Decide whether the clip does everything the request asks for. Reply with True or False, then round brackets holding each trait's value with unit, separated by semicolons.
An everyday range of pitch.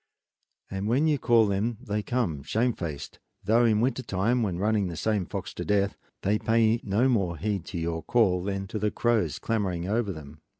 True (3.9 semitones)